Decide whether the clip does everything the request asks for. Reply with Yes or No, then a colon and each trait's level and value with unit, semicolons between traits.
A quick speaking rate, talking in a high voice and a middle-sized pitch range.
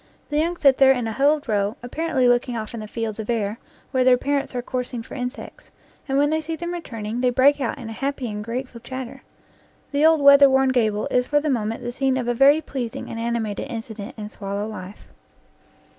Yes: fast, 225 wpm; very high, 250 Hz; average, 3.8 semitones